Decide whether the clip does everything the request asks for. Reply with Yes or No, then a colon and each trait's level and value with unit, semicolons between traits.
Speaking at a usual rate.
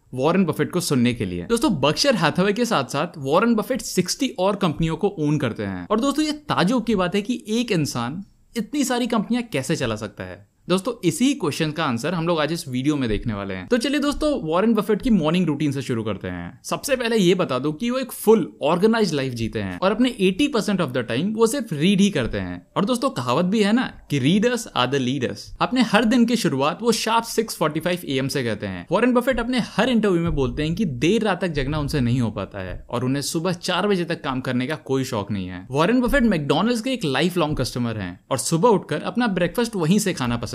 No: fast, 240 wpm